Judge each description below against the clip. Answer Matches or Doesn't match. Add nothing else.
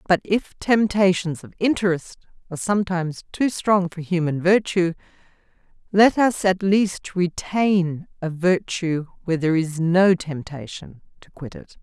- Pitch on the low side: Doesn't match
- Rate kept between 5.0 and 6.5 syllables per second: Doesn't match